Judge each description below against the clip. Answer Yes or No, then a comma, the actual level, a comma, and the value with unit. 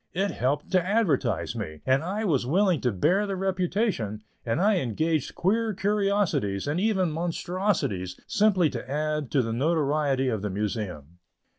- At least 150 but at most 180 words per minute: Yes, average, 155 wpm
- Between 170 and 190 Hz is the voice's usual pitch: No, medium, 155 Hz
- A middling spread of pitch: No, wide, 7.8 semitones